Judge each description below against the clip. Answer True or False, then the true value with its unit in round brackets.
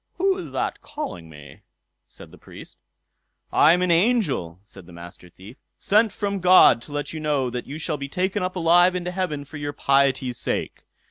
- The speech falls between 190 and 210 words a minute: True (195 wpm)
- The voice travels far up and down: True (6.6 semitones)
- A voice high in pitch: False (150 Hz)